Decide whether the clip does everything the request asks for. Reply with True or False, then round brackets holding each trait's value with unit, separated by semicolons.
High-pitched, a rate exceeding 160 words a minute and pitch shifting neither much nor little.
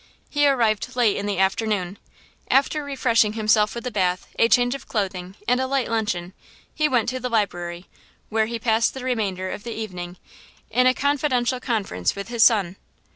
True (225 Hz; 180 wpm; 4.2 semitones)